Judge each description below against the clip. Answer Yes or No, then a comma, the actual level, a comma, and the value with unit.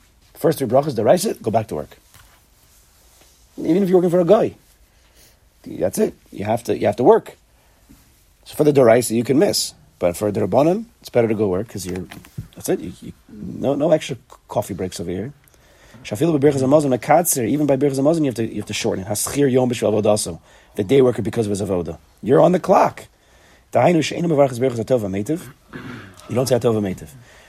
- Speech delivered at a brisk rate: No, average, 175 wpm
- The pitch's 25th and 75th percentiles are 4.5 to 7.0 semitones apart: Yes, wide, 5.5 semitones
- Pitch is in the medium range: No, low, 120 Hz